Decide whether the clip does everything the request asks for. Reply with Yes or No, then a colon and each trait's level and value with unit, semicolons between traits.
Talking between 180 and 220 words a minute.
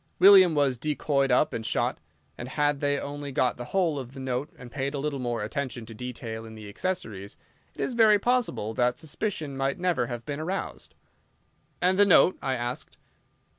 Yes: average, 190 wpm